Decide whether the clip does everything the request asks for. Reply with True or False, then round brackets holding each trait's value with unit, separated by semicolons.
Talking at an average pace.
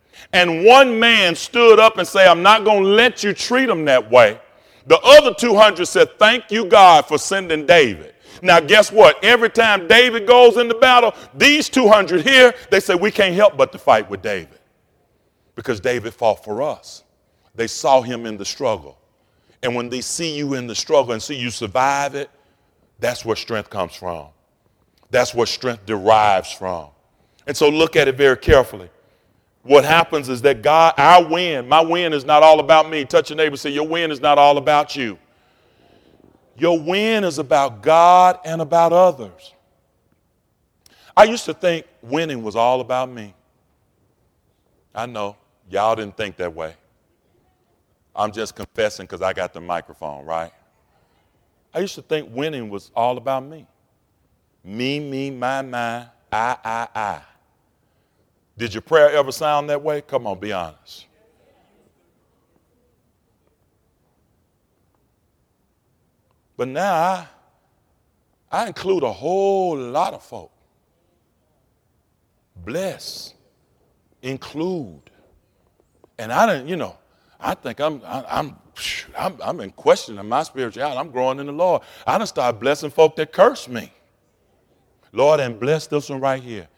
True (155 wpm)